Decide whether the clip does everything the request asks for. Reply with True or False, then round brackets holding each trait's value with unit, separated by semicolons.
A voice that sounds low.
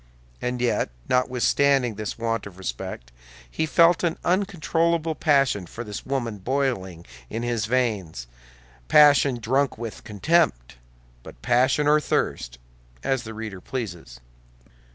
True (120 Hz)